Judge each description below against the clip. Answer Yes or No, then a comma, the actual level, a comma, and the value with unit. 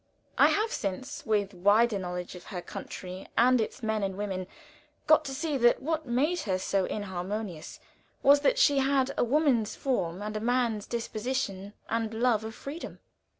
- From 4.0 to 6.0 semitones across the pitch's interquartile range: Yes, average, 5.1 semitones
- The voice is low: No, high, 220 Hz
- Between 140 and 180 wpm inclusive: Yes, average, 170 wpm